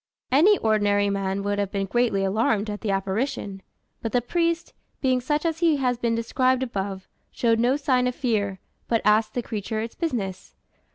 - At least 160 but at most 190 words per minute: Yes, average, 180 wpm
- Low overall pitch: No, high, 225 Hz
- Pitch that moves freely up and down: No, average, 4.1 semitones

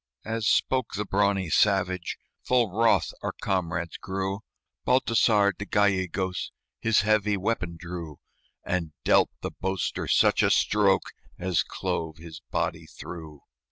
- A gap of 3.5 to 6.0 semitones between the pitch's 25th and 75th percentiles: No, average, 3.0 semitones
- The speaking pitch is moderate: No, very low, 95 Hz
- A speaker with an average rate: No, slow, 125 wpm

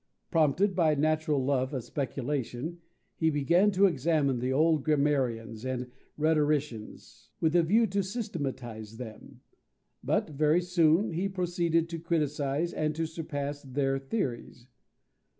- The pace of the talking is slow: Yes, slow, 130 wpm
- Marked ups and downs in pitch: No, average, 3.9 semitones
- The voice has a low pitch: No, medium, 150 Hz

